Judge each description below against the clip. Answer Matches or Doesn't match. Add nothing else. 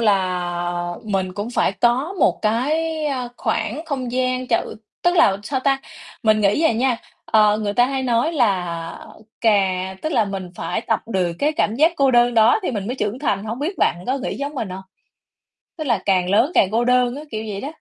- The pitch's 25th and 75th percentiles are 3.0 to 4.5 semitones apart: Doesn't match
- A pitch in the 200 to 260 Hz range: Matches